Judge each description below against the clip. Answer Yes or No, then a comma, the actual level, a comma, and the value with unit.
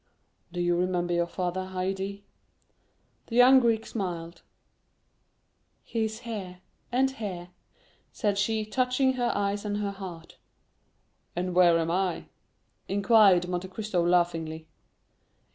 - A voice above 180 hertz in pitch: Yes, high, 190 Hz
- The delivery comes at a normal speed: No, slow, 125 wpm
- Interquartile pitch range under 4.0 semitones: Yes, average, 3.6 semitones